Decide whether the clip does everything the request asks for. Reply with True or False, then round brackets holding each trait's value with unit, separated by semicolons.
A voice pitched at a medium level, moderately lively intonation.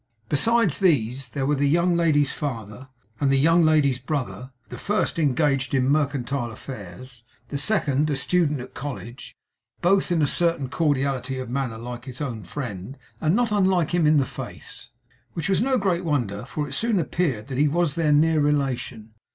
True (145 Hz; 4.3 semitones)